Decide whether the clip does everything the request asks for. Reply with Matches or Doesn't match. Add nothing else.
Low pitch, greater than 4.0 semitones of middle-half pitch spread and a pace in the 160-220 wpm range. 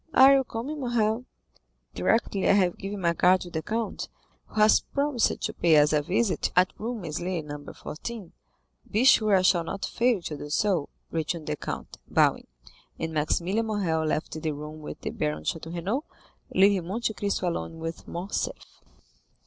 Doesn't match